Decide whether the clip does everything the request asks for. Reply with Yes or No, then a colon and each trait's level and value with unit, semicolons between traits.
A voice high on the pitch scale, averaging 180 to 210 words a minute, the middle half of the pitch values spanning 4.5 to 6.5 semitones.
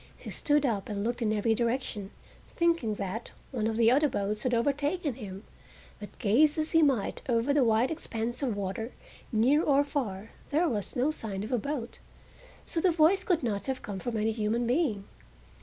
Yes: high, 240 Hz; average, 190 wpm; average, 5.2 semitones